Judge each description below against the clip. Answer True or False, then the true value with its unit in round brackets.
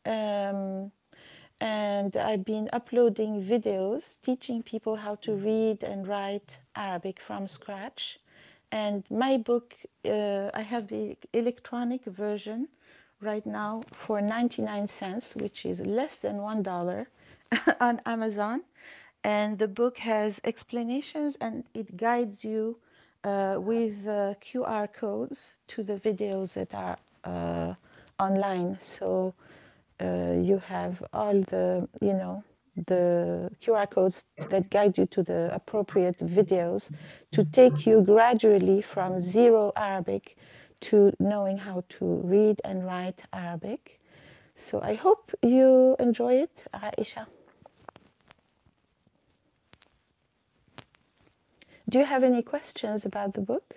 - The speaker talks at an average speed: True (120 wpm)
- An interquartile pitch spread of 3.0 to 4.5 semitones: True (3.4 semitones)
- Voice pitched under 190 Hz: False (210 Hz)